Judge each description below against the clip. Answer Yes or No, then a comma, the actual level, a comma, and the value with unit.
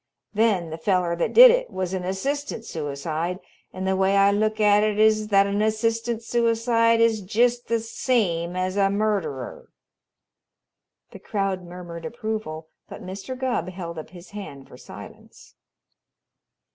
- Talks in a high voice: Yes, high, 200 Hz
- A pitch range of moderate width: Yes, average, 4.0 semitones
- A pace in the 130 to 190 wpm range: Yes, average, 150 wpm